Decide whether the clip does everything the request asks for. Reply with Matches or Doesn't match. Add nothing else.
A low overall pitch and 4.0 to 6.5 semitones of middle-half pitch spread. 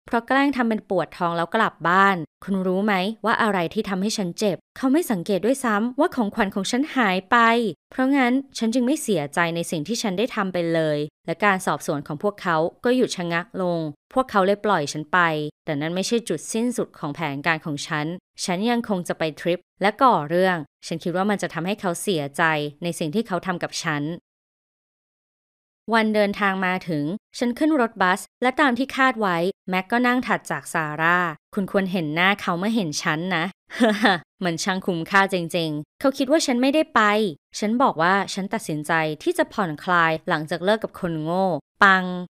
Doesn't match